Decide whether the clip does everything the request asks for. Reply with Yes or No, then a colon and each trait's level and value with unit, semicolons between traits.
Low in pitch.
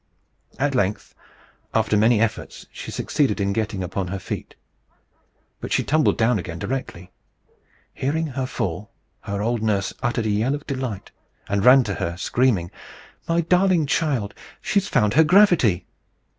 Yes: low, 115 Hz